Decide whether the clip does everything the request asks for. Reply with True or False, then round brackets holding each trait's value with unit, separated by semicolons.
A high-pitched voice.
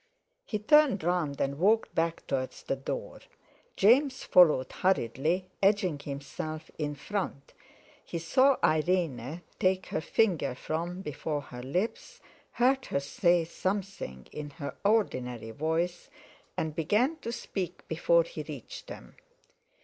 False (170 Hz)